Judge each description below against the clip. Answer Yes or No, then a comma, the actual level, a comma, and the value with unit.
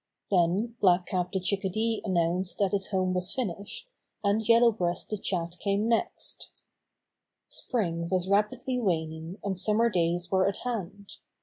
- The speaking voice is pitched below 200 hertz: Yes, high, 190 Hz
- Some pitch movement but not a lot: Yes, average, 3.2 semitones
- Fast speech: No, average, 145 wpm